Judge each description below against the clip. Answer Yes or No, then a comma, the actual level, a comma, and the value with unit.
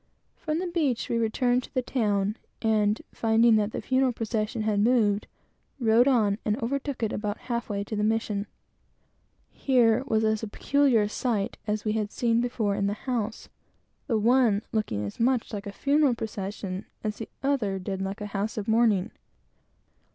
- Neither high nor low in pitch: No, high, 220 Hz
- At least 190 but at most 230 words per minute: No, average, 175 wpm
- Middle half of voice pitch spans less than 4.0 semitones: Yes, average, 2.9 semitones